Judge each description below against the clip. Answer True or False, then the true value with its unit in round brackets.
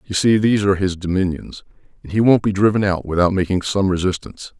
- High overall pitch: False (95 Hz)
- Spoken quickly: True (210 wpm)